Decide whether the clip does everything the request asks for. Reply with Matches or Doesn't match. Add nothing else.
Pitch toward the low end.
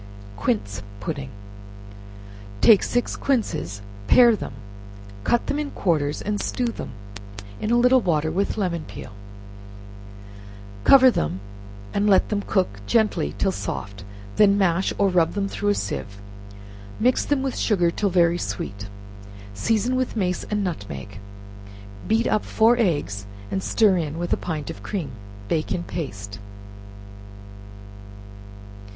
Doesn't match